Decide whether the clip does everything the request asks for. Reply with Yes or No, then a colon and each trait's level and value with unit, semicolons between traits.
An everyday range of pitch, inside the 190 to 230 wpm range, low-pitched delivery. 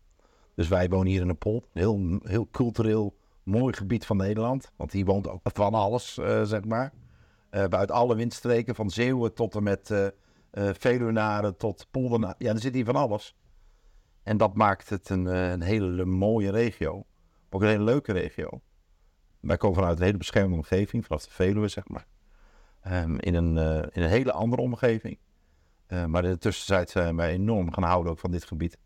Yes: average, 3.7 semitones; average, 195 wpm; low, 100 Hz